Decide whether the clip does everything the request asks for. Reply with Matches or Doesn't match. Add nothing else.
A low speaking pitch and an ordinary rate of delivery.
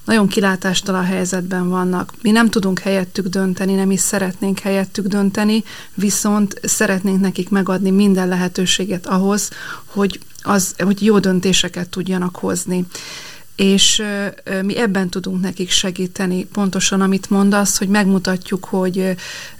Doesn't match